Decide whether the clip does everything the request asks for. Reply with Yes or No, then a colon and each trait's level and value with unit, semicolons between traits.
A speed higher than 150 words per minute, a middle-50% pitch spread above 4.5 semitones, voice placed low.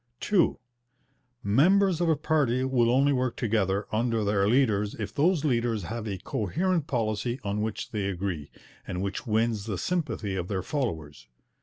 Yes: average, 160 wpm; average, 5.3 semitones; low, 115 Hz